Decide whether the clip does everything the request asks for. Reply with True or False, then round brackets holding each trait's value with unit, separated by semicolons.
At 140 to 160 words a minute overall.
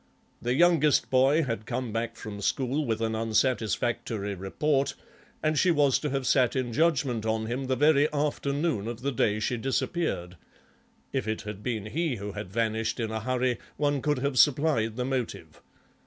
False (170 wpm)